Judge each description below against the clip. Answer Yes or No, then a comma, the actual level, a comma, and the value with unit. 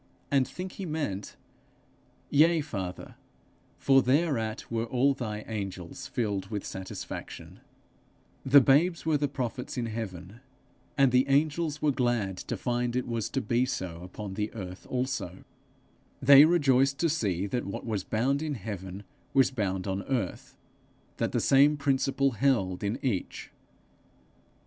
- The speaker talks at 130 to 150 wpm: Yes, average, 145 wpm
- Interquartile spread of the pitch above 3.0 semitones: Yes, wide, 5.4 semitones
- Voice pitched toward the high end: No, low, 125 Hz